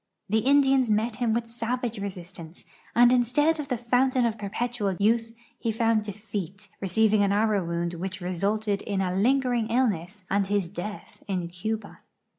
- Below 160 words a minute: No, average, 165 wpm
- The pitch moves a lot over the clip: No, average, 3.5 semitones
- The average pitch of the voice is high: Yes, high, 215 Hz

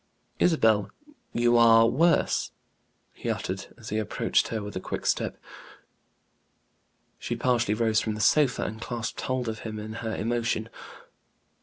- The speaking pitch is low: Yes, low, 115 Hz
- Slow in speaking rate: No, average, 145 wpm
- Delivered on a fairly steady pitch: Yes, narrow, 1.7 semitones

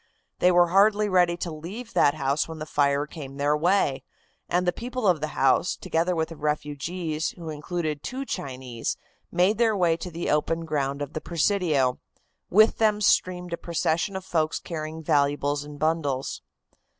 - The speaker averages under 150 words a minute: No, average, 175 wpm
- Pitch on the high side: No, medium, 160 Hz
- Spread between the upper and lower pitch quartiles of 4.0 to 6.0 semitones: No, average, 3.5 semitones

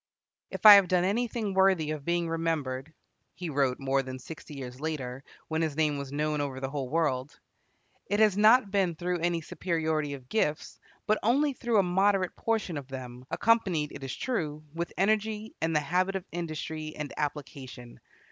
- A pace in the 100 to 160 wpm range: No, average, 180 wpm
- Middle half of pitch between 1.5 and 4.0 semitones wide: No, average, 5.2 semitones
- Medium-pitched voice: Yes, medium, 160 Hz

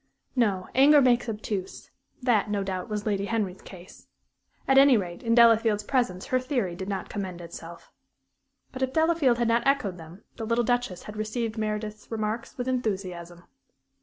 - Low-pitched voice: No, high, 215 Hz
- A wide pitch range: No, average, 4.2 semitones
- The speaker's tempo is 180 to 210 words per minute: No, average, 165 wpm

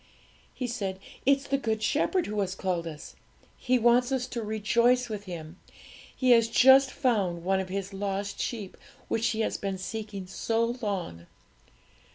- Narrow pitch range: No, average, 4.2 semitones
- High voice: Yes, high, 215 Hz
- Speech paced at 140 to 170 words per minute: Yes, average, 165 wpm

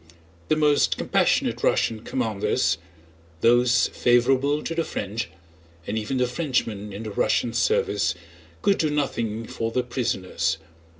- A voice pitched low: Yes, low, 115 Hz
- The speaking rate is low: Yes, slow, 120 wpm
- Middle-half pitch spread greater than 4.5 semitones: Yes, average, 5.0 semitones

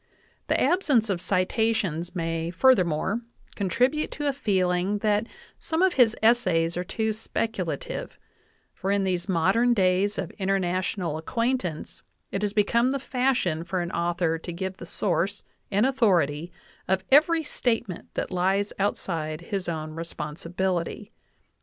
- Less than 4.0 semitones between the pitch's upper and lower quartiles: No, average, 4.6 semitones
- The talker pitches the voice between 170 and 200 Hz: Yes, high, 190 Hz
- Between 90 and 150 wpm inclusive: Yes, average, 140 wpm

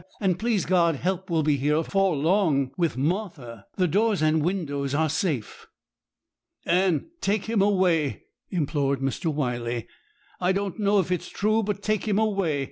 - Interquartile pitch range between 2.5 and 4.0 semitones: No, average, 5.2 semitones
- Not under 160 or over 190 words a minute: Yes, average, 165 wpm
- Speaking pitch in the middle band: Yes, medium, 175 Hz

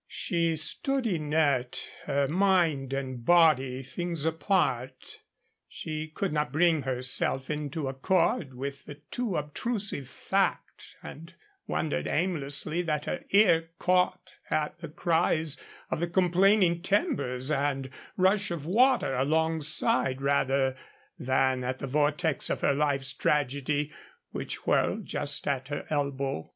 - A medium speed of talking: No, slow, 125 wpm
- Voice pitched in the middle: Yes, medium, 150 Hz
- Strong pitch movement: No, average, 4.0 semitones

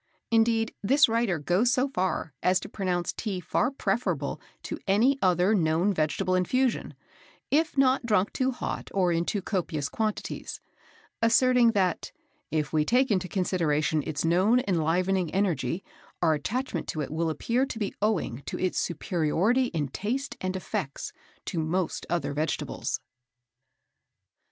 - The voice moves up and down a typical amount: No, wide, 5.8 semitones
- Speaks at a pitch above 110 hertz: Yes, medium, 185 Hz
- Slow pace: No, average, 145 wpm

